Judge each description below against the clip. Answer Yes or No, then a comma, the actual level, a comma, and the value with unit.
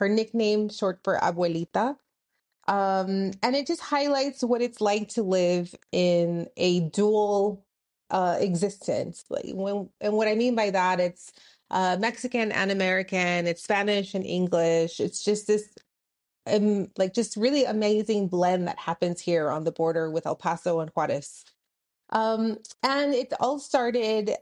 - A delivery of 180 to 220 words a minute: No, average, 150 wpm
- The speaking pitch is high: Yes, high, 200 Hz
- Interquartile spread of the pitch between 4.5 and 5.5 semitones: No, average, 3.8 semitones